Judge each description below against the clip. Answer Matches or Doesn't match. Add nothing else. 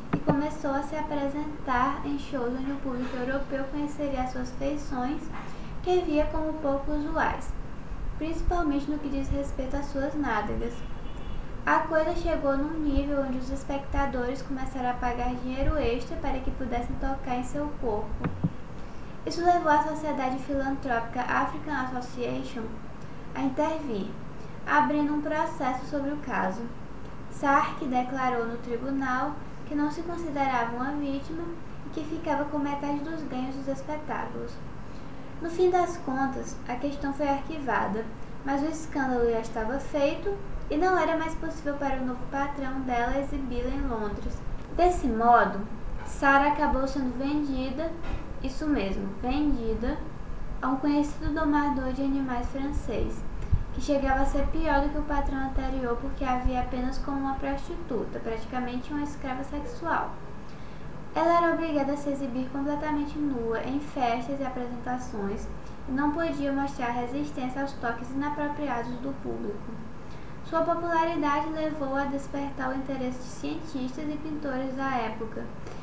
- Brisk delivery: Doesn't match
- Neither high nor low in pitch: Doesn't match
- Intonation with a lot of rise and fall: Doesn't match